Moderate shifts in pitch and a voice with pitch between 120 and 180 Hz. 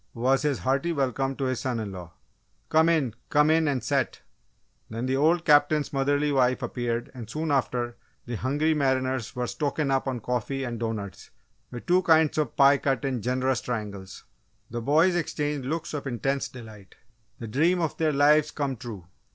Yes: average, 3.6 semitones; low, 135 Hz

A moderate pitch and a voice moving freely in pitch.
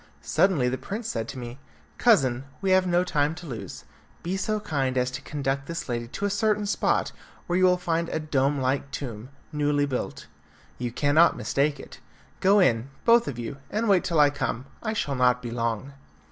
Yes: medium, 145 Hz; wide, 6.0 semitones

